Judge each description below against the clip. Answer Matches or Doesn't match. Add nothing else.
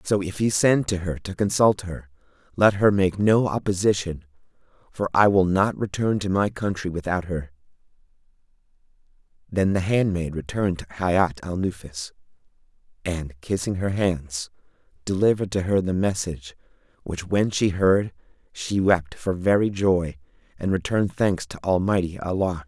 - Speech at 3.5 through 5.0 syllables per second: Matches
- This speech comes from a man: Matches